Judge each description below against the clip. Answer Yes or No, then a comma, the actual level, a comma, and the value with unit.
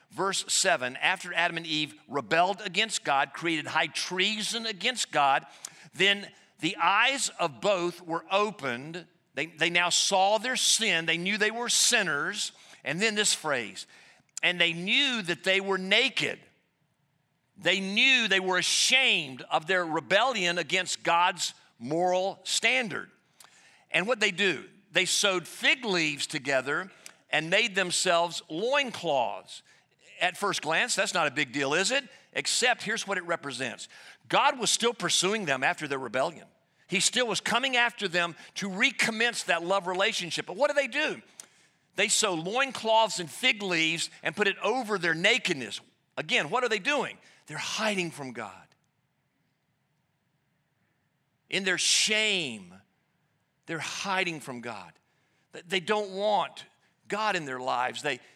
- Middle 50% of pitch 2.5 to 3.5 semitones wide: No, average, 4.5 semitones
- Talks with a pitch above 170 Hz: Yes, medium, 185 Hz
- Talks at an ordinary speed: Yes, average, 145 wpm